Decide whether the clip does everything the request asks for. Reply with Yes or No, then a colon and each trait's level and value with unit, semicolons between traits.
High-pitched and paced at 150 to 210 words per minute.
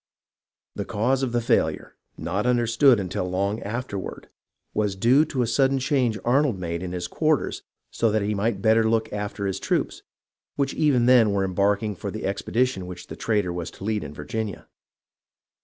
No: low, 110 Hz; average, 175 wpm